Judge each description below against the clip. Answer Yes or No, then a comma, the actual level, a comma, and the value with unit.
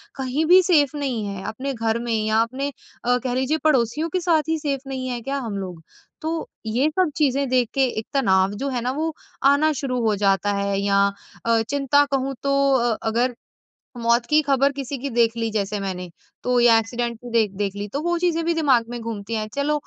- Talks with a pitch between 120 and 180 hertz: No, very high, 250 Hz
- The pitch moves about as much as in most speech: Yes, average, 4.1 semitones